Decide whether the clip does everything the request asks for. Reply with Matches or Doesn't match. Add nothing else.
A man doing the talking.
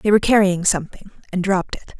Doesn't match